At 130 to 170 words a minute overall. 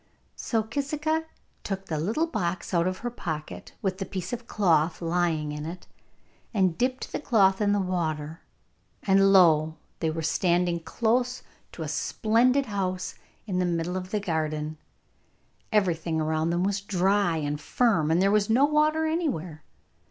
Yes: average, 160 wpm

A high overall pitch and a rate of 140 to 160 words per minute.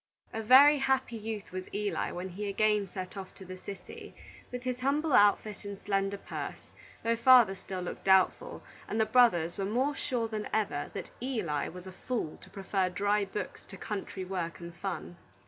No: high, 205 Hz; average, 185 wpm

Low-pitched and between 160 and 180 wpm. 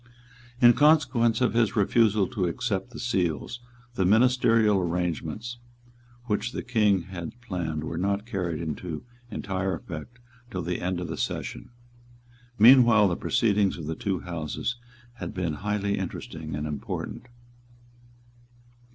No: low, 100 Hz; slow, 135 wpm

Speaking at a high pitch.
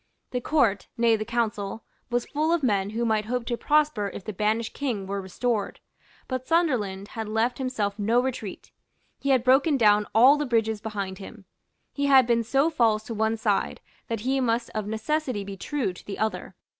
Yes: high, 225 Hz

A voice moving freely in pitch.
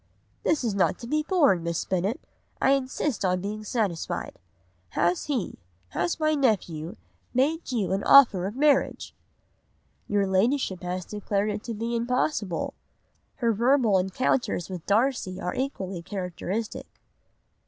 Yes: wide, 5.9 semitones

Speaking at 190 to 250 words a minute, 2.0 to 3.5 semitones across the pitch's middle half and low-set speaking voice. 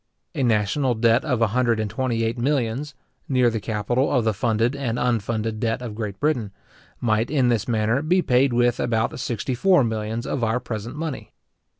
Yes: average, 195 wpm; narrow, 2.5 semitones; low, 120 Hz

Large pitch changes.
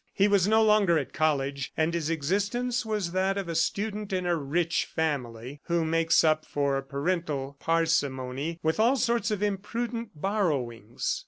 Yes: wide, 6.0 semitones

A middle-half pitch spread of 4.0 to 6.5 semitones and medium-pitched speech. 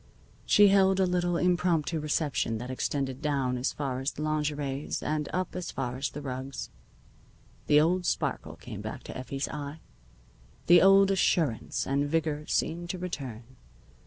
Yes: average, 4.5 semitones; medium, 150 Hz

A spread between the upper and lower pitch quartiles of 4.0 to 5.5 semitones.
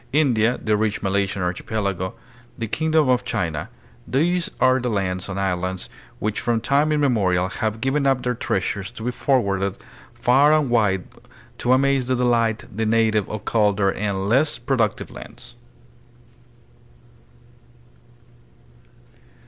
Yes: average, 4.7 semitones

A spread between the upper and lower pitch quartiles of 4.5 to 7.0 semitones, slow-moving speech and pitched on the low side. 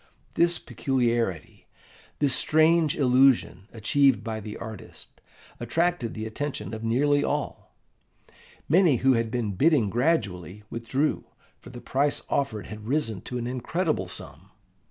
Yes: average, 4.8 semitones; slow, 130 wpm; low, 125 Hz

